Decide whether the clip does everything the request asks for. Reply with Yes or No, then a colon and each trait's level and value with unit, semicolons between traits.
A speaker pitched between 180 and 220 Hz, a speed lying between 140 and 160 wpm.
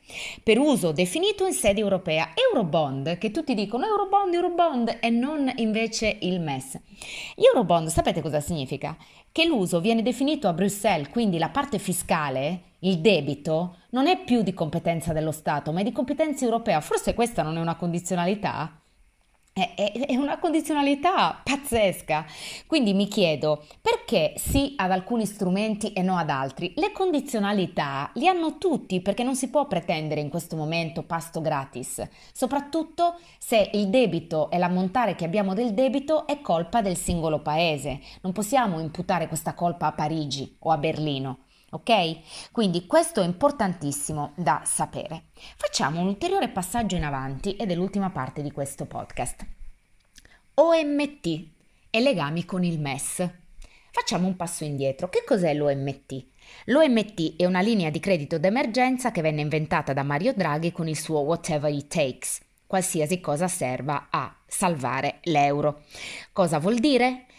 Yes: medium, 185 Hz; average, 150 wpm